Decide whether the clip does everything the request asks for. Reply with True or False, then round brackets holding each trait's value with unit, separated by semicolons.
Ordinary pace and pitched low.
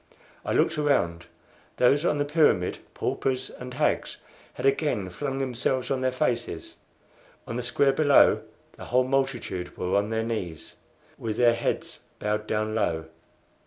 True (150 wpm; 125 Hz)